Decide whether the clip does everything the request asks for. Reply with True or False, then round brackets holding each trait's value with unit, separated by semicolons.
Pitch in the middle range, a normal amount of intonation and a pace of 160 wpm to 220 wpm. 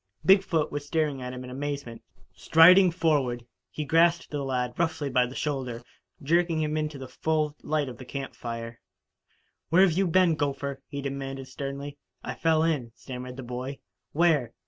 True (145 Hz; 3.7 semitones; 170 wpm)